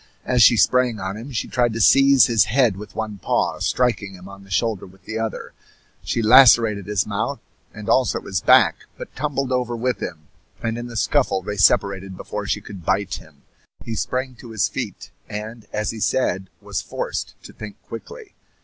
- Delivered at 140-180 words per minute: No, average, 195 wpm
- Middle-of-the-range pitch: No, low, 110 Hz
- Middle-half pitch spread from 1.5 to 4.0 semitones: Yes, average, 3.7 semitones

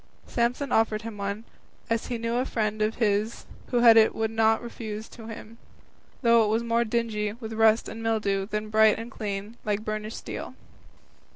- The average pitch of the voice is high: Yes, high, 220 Hz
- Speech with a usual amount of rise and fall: No, narrow, 1.4 semitones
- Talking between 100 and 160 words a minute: No, average, 190 wpm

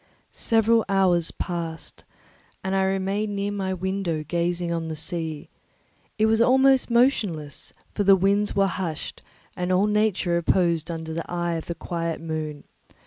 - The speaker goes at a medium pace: Yes, average, 150 wpm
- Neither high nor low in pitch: Yes, medium, 180 Hz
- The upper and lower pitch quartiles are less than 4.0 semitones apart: Yes, average, 3.4 semitones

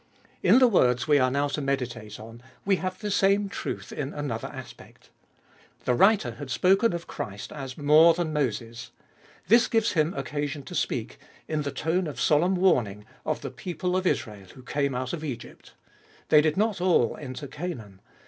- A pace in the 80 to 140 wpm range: No, average, 180 wpm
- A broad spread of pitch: Yes, wide, 6.1 semitones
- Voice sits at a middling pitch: Yes, medium, 145 Hz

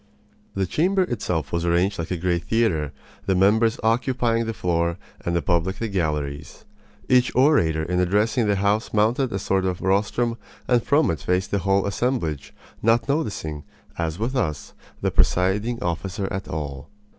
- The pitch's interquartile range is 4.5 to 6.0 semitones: Yes, average, 5.2 semitones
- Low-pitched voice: Yes, very low, 95 Hz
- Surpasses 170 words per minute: No, average, 165 wpm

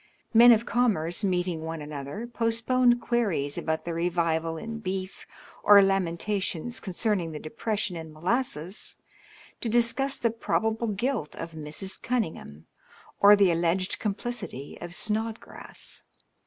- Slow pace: Yes, slow, 125 wpm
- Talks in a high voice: Yes, high, 195 Hz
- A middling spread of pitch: No, wide, 5.7 semitones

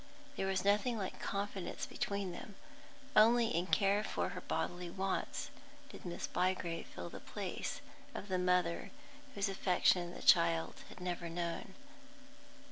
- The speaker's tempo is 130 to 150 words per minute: Yes, average, 140 wpm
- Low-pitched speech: No, medium, 185 Hz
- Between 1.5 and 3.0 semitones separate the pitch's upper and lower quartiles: Yes, narrow, 2.4 semitones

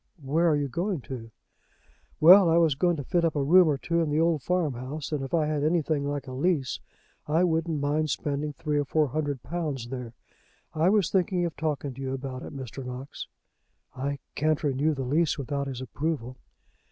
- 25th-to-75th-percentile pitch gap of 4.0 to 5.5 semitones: No, average, 3.3 semitones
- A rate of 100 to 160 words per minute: No, average, 200 wpm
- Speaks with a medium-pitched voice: Yes, medium, 150 Hz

